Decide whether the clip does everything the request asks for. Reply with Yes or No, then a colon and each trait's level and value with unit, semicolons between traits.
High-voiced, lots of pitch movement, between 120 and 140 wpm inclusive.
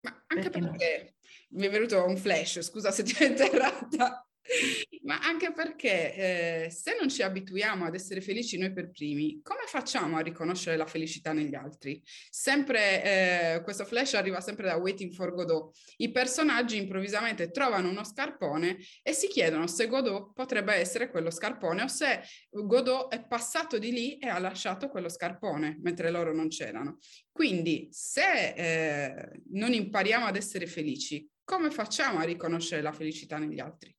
No: high, 195 Hz; wide, 6.7 semitones; average, 160 wpm